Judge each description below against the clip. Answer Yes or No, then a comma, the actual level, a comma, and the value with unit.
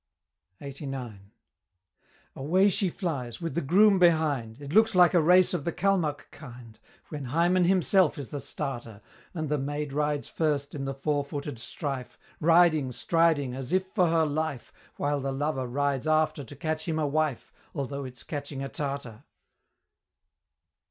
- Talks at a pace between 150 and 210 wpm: Yes, average, 155 wpm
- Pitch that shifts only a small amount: No, average, 3.4 semitones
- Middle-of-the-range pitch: Yes, medium, 145 Hz